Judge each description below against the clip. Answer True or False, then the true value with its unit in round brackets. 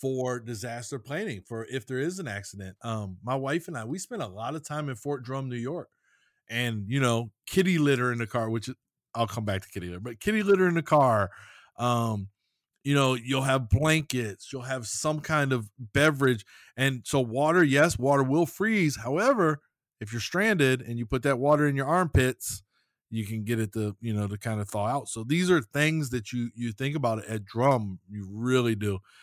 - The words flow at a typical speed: False (215 wpm)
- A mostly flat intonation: False (4.5 semitones)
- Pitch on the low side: True (130 Hz)